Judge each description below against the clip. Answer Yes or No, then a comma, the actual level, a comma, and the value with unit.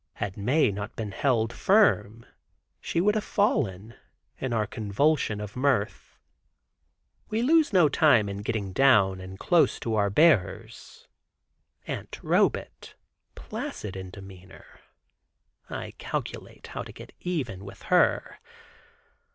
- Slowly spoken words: Yes, slow, 125 wpm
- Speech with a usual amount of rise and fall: No, wide, 7.4 semitones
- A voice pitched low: Yes, low, 110 Hz